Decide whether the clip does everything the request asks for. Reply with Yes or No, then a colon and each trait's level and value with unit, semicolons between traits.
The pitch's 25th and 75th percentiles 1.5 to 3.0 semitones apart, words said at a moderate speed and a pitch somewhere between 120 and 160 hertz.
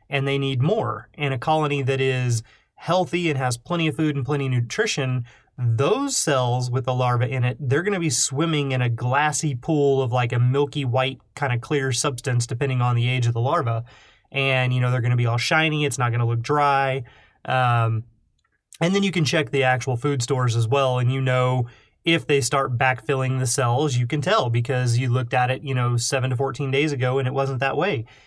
No: narrow, 2.6 semitones; fast, 225 wpm; low, 130 Hz